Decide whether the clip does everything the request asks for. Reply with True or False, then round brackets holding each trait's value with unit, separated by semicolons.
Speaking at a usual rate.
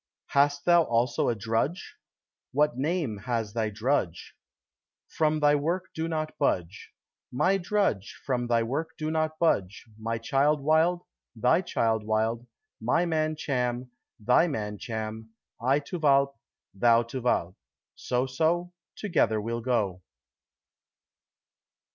False (130 wpm)